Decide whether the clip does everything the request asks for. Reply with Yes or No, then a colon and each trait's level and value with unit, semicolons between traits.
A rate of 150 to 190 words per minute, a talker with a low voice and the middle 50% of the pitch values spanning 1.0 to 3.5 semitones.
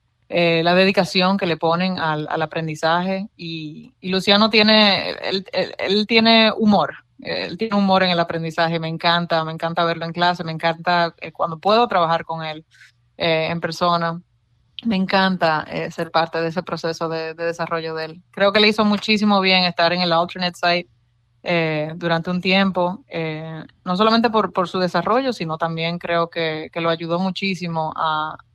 No: average, 180 wpm; medium, 170 Hz; narrow, 2.6 semitones